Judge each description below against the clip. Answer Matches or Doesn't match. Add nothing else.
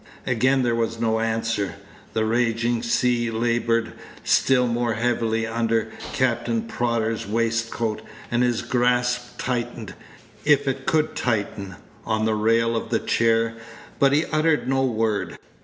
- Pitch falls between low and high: Doesn't match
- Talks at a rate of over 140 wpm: Doesn't match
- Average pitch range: Doesn't match